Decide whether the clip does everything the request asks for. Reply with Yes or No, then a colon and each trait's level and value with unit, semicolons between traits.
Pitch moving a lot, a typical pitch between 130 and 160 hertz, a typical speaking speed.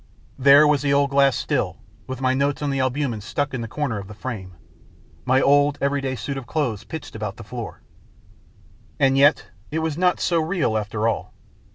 No: average, 3.7 semitones; low, 135 Hz; average, 195 wpm